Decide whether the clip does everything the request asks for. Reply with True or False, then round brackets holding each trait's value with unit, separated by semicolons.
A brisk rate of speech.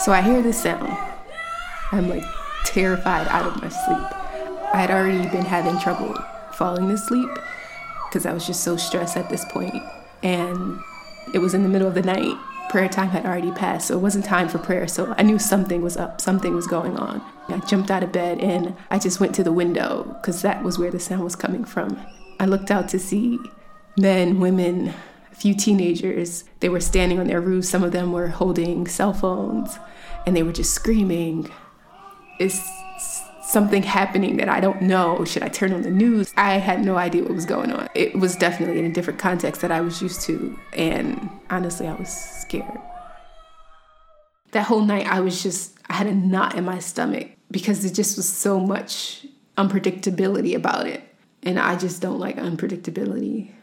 False (195 wpm)